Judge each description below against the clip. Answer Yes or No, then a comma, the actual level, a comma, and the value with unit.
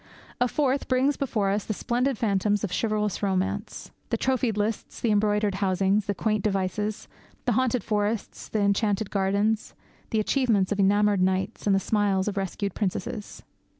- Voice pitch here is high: Yes, high, 210 Hz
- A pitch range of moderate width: No, narrow, 2.1 semitones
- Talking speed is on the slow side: No, average, 160 wpm